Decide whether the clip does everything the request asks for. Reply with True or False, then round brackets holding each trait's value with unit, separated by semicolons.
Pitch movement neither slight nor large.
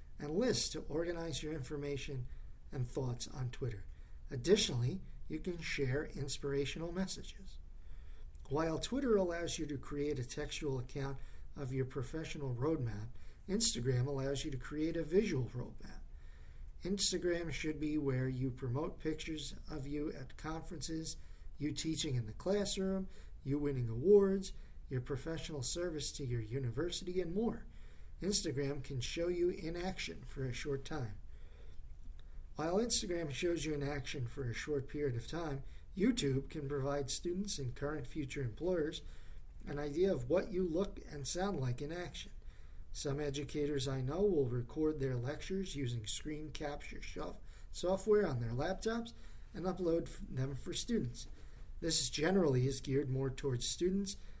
True (4.5 semitones)